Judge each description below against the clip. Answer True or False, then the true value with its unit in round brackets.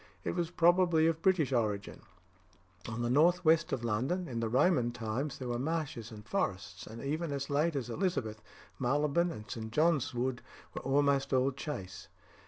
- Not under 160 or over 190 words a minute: True (175 wpm)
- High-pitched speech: False (135 Hz)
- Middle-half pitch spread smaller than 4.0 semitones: False (5.6 semitones)